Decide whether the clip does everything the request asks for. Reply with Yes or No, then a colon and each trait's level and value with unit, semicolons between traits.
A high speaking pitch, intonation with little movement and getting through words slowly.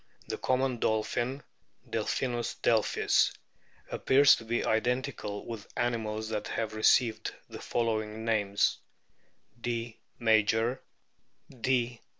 No: low, 115 Hz; narrow, 1.8 semitones; slow, 100 wpm